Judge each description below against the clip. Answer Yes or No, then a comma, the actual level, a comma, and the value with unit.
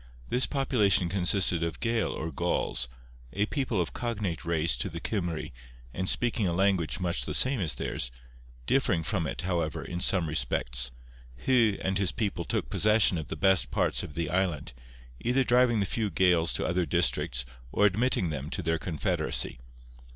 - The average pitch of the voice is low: Yes, very low, 90 Hz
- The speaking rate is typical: Yes, average, 175 wpm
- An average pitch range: Yes, average, 4.5 semitones